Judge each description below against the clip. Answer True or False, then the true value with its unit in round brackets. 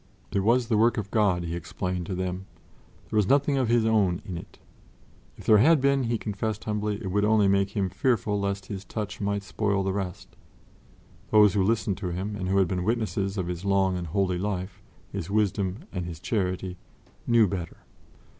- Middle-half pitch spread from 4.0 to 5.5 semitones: False (2.6 semitones)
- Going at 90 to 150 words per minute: False (200 wpm)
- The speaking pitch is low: True (100 Hz)